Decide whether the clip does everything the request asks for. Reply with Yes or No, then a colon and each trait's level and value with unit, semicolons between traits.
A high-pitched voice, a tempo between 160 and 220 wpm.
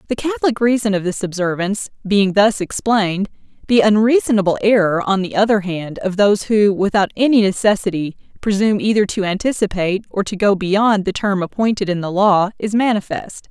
Yes: high, 205 Hz; average, 170 wpm